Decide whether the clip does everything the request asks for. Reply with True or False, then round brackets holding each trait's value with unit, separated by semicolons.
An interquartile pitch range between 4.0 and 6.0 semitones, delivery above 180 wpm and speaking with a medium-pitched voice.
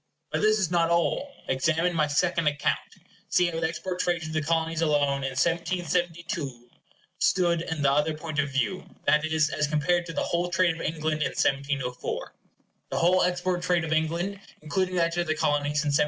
False (2.8 semitones; 195 wpm; 160 Hz)